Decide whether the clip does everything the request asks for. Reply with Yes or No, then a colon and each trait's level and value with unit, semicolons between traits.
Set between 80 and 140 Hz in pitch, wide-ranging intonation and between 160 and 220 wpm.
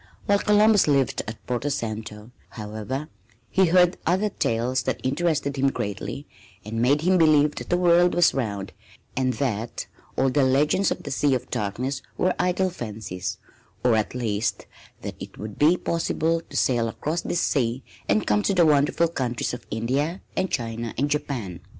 Yes: low, 135 Hz; wide, 6.5 semitones; average, 170 wpm